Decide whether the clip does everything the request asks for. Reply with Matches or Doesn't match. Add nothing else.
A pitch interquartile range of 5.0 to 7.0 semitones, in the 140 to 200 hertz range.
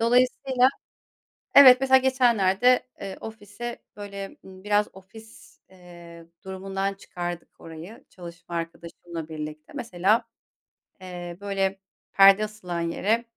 Doesn't match